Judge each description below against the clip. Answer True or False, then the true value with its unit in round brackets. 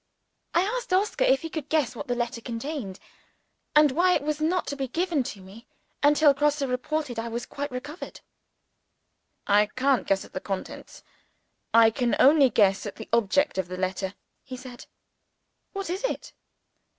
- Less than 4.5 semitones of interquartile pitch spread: False (5.0 semitones)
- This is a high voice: True (265 Hz)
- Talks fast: False (175 wpm)